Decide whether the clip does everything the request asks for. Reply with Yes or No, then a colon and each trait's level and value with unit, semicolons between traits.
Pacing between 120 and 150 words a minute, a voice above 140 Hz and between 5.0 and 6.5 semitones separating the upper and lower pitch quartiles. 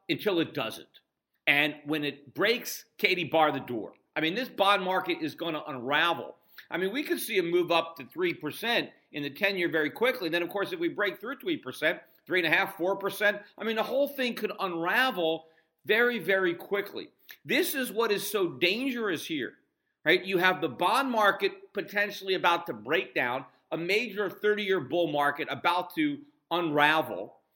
No: average, 180 wpm; high, 190 Hz; wide, 5.4 semitones